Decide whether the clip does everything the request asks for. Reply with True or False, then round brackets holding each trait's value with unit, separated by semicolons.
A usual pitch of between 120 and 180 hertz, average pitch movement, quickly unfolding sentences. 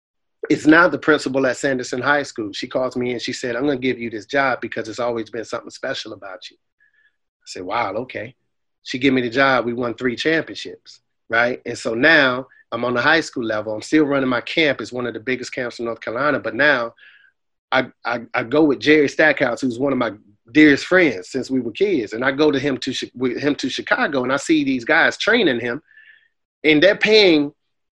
True (135 Hz; 4.1 semitones; 225 wpm)